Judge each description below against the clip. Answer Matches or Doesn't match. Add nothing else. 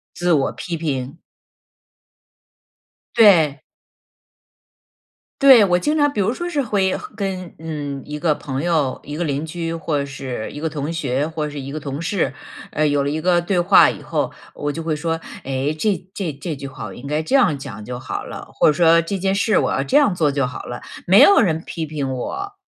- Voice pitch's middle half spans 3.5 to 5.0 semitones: Matches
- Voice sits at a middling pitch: Matches